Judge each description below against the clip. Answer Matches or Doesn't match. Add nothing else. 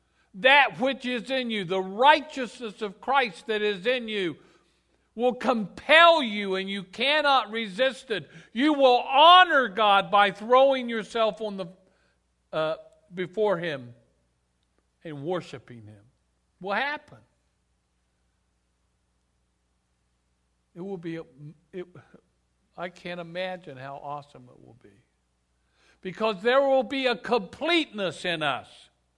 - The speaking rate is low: Matches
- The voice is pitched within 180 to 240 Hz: Matches